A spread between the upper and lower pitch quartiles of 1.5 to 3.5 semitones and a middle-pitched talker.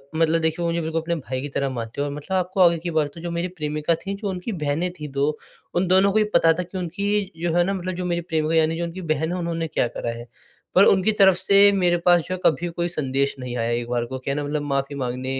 No: average, 4.0 semitones; medium, 165 Hz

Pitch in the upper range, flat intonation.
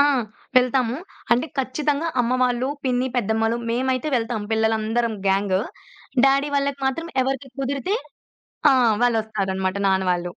No: high, 245 Hz; average, 3.5 semitones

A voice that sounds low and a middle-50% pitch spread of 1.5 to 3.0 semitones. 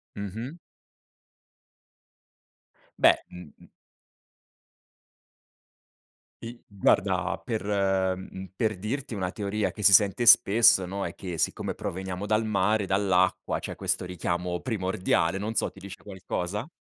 Yes: low, 100 Hz; average, 2.7 semitones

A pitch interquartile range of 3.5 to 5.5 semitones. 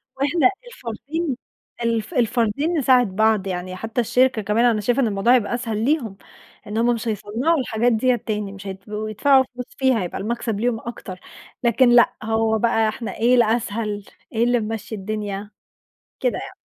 No: average, 2.7 semitones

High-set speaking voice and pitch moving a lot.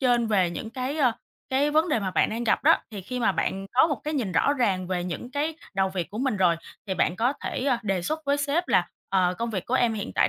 Yes: high, 230 Hz; wide, 6.4 semitones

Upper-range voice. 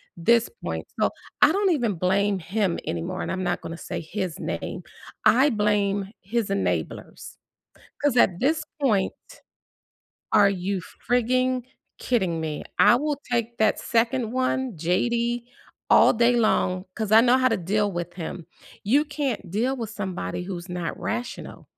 Yes: high, 215 Hz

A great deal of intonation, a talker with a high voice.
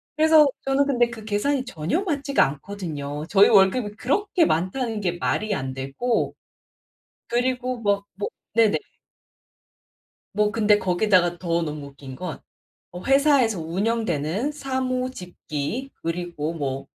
Yes: wide, 7.2 semitones; high, 205 Hz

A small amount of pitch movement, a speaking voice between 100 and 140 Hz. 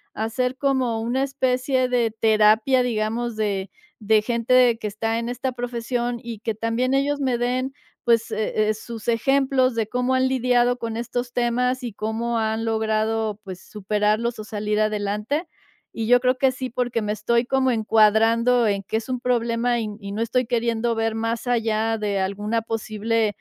No: narrow, 2.3 semitones; high, 230 Hz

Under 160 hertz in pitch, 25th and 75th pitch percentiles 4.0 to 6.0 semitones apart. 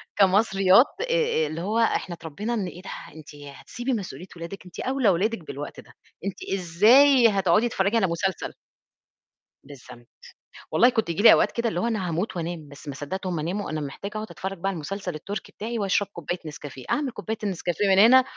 No: high, 190 Hz; average, 4.6 semitones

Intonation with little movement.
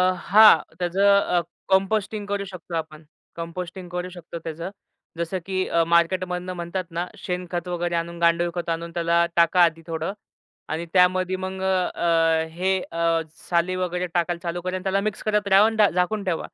Yes: narrow, 1.9 semitones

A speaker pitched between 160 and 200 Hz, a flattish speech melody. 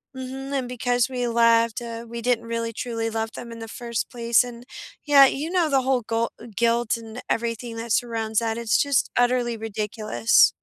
No: high, 235 Hz; narrow, 1.4 semitones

